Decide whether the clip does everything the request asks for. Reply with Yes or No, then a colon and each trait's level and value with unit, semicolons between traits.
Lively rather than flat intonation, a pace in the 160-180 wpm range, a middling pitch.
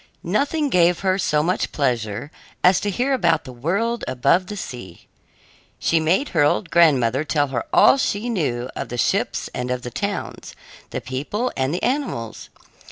Yes: wide, 7.8 semitones; average, 170 wpm; medium, 165 Hz